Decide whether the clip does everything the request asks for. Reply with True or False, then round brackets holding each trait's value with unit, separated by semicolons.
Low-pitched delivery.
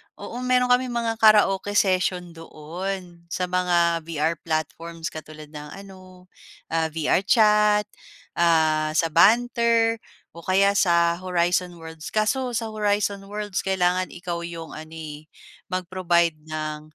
False (180 Hz)